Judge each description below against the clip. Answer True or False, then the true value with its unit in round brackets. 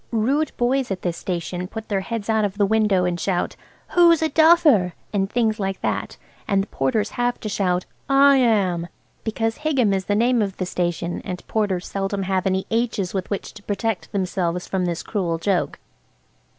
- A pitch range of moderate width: True (3.7 semitones)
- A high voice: True (200 Hz)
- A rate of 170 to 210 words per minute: True (190 wpm)